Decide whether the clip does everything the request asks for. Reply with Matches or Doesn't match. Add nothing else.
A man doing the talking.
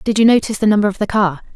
Doesn't match